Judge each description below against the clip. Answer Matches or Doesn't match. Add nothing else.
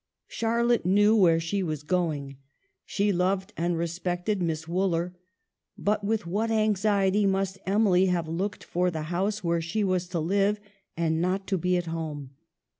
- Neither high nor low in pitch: Matches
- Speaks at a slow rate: Doesn't match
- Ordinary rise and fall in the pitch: Matches